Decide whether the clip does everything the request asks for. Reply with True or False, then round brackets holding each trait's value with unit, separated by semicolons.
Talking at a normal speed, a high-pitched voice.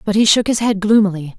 False (260 wpm; 205 Hz)